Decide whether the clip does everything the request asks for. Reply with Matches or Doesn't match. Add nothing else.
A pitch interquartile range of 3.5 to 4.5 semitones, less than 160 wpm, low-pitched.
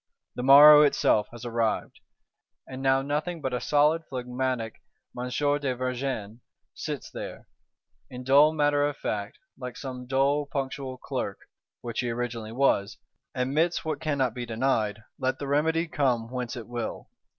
Doesn't match